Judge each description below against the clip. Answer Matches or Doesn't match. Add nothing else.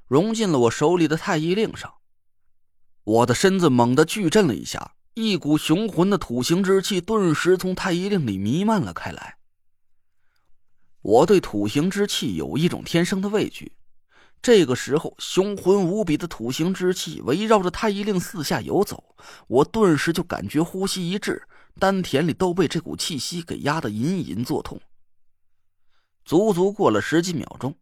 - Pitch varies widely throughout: Matches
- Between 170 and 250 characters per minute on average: Matches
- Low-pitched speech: Doesn't match